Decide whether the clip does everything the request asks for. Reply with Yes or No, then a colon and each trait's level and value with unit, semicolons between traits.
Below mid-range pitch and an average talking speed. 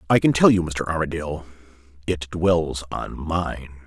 Yes: very low, 80 Hz; average, 155 wpm